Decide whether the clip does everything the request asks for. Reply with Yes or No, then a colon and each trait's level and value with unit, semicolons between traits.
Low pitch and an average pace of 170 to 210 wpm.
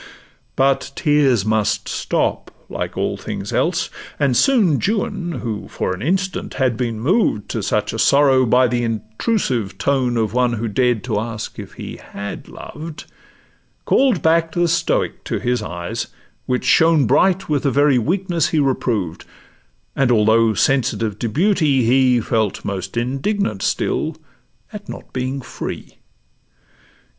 No: low, 130 Hz; average, 145 wpm